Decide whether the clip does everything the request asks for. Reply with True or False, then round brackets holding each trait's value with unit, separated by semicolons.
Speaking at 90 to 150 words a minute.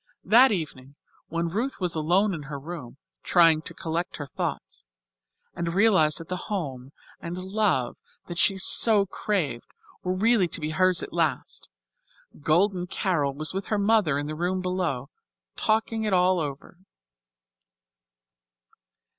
True (145 wpm)